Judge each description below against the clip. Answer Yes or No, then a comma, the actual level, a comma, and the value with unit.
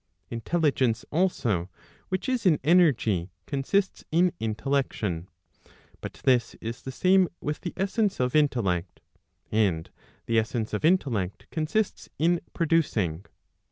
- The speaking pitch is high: No, low, 135 Hz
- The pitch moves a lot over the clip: Yes, wide, 7.9 semitones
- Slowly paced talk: Yes, slow, 120 wpm